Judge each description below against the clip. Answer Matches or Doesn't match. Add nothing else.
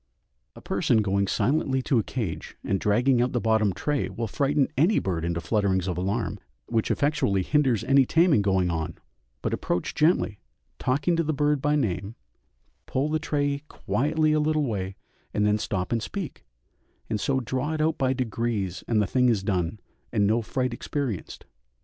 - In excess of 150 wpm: Matches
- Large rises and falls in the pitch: Matches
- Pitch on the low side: Matches